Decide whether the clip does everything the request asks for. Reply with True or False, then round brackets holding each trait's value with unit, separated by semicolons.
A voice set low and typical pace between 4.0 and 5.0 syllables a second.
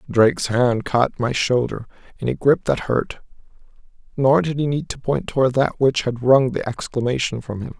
True (125 Hz; 4.9 syllables/s)